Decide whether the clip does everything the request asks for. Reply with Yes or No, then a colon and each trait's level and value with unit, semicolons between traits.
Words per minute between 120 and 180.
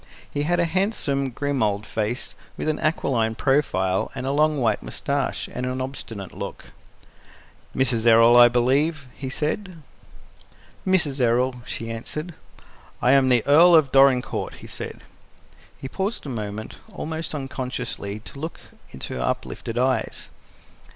Yes: average, 140 wpm